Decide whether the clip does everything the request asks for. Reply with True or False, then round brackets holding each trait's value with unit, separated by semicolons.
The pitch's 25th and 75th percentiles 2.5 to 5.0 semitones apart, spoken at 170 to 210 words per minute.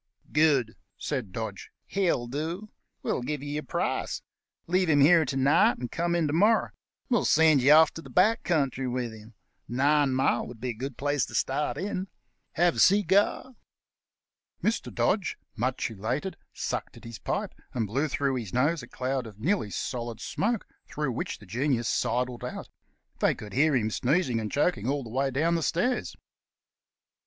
False (5.5 semitones; 180 wpm)